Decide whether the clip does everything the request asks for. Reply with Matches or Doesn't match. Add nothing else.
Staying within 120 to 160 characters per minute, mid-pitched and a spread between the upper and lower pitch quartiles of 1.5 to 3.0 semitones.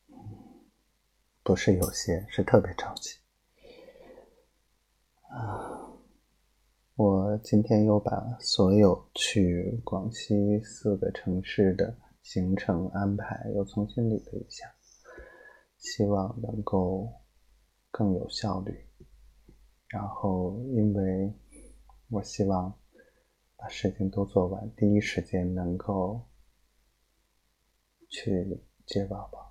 Doesn't match